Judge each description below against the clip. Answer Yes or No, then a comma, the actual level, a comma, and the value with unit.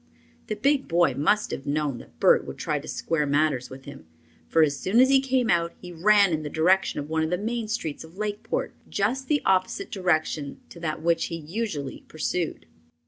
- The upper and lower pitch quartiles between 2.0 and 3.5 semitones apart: No, wide, 5.5 semitones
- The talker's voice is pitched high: No, medium, 170 Hz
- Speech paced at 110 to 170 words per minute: No, fast, 205 wpm